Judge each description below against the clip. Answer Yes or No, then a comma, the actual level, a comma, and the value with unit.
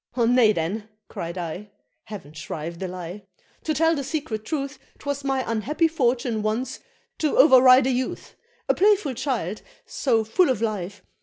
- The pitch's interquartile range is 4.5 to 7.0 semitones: Yes, average, 5.2 semitones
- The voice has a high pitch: Yes, high, 235 Hz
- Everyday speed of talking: Yes, average, 160 wpm